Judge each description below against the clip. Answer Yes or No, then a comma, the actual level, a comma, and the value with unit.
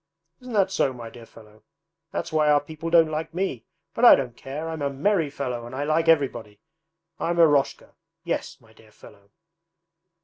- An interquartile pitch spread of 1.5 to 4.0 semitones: No, wide, 5.5 semitones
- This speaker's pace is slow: No, average, 180 wpm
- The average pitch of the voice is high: No, medium, 145 Hz